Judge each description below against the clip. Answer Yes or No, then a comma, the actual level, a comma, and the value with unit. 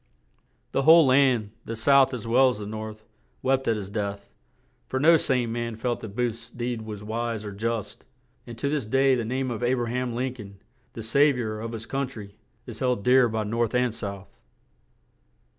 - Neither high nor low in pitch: No, low, 120 Hz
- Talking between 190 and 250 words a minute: Yes, average, 200 wpm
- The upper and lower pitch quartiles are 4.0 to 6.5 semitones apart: No, average, 2.9 semitones